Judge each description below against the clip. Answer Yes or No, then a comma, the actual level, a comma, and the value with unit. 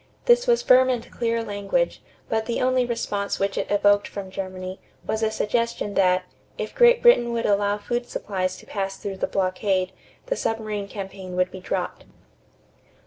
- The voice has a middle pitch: No, high, 205 Hz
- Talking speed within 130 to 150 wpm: No, average, 170 wpm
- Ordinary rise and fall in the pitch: Yes, average, 3.6 semitones